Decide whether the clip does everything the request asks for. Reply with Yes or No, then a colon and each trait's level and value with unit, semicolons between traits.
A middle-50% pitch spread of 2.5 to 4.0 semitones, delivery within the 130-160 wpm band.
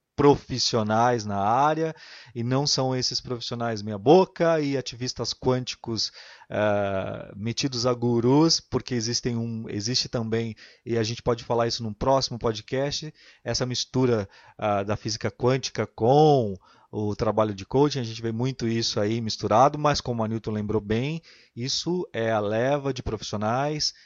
Yes: average, 3.3 semitones; average, 150 wpm